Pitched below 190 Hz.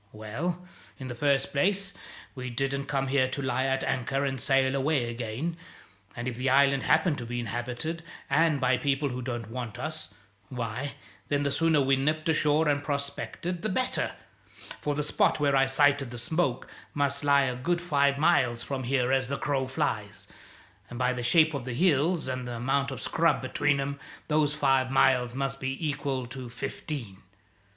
Yes: low, 135 Hz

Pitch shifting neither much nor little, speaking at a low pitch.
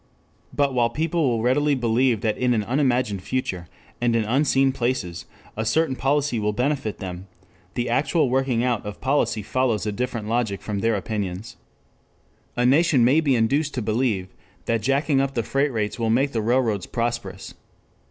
Yes: average, 3.6 semitones; low, 120 Hz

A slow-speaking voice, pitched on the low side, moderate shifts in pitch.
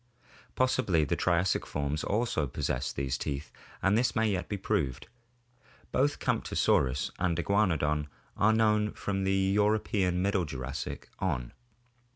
No: slow, 130 wpm; very low, 95 Hz; wide, 6.2 semitones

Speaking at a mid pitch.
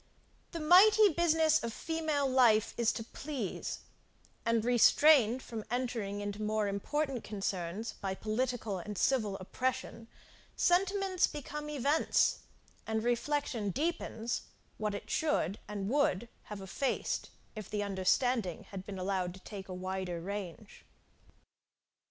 No: high, 225 Hz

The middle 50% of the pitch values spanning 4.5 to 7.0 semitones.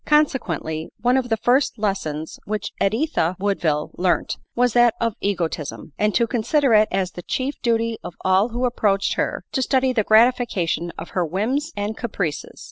Yes: average, 5.0 semitones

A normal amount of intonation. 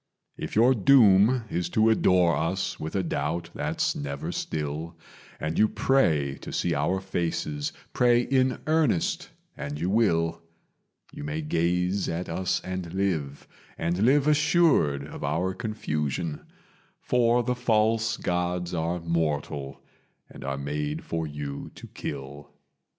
No: wide, 6.4 semitones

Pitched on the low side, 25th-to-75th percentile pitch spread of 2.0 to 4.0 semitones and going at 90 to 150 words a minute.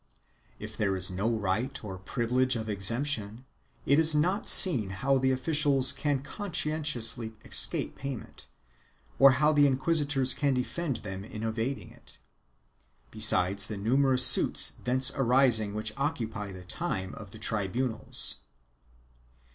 No: low, 125 Hz; average, 4.6 semitones; average, 140 wpm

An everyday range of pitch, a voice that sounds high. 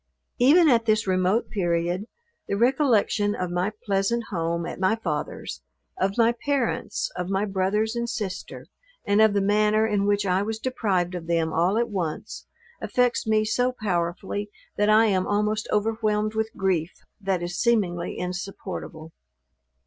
Yes: average, 3.2 semitones; high, 205 Hz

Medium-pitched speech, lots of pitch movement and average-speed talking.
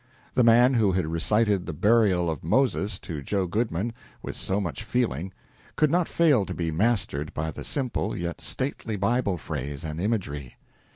No: low, 100 Hz; wide, 5.9 semitones; average, 170 wpm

